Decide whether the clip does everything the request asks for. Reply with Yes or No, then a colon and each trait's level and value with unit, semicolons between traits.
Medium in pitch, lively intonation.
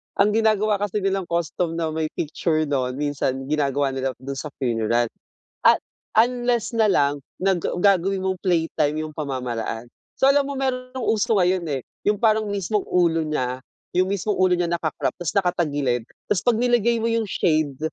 Yes: medium, 175 Hz; wide, 6.4 semitones